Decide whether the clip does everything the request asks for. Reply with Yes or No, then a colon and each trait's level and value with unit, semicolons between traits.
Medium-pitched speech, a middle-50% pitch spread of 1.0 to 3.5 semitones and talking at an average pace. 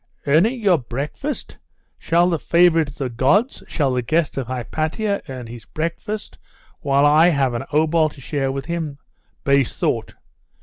No: medium, 150 Hz; average, 4.0 semitones; average, 160 wpm